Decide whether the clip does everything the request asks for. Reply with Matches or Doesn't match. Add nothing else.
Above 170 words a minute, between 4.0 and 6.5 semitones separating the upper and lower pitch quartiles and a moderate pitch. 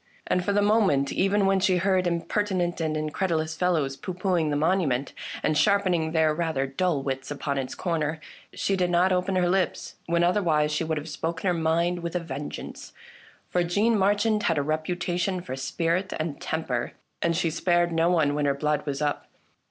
Doesn't match